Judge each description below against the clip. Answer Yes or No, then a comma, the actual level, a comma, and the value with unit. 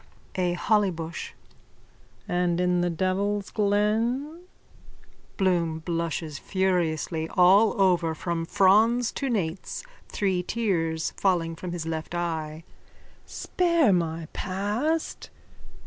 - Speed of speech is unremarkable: No, slow, 100 wpm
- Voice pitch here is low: No, medium, 180 Hz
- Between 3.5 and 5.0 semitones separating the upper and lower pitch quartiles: Yes, average, 3.8 semitones